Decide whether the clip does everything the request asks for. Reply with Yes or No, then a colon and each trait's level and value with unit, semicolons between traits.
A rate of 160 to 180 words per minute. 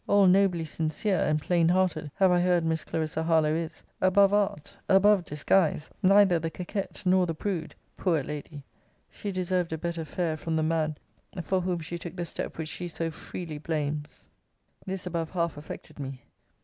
Yes: average, 175 wpm